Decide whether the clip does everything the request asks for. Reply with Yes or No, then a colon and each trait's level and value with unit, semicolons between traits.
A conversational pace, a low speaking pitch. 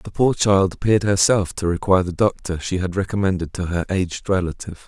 Yes: average, 195 wpm; very low, 95 Hz